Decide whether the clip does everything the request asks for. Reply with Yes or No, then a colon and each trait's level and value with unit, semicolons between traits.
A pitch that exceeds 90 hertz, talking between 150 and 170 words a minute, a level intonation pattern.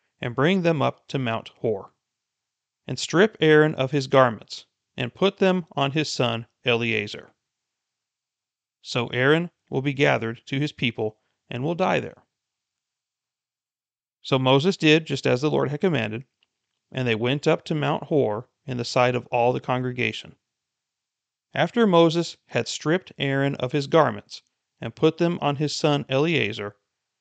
No: low, 135 Hz; average, 155 wpm; average, 4.2 semitones